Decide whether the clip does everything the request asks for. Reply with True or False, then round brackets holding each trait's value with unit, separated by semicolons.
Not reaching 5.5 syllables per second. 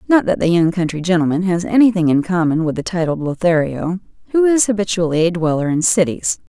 False (5.9 syllables/s)